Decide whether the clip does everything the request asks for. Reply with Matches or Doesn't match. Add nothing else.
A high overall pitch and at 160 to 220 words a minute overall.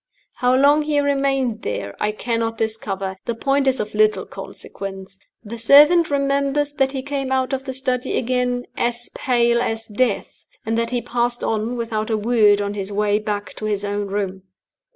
Matches